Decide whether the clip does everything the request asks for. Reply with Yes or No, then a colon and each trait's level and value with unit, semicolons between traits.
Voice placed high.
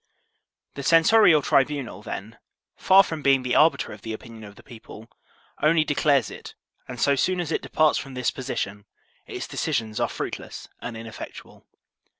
No: low, 135 Hz